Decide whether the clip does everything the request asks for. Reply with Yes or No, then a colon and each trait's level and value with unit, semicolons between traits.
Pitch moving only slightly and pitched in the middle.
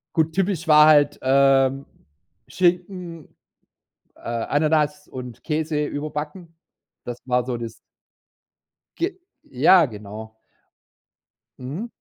No: average, 4.3 semitones; medium, 150 Hz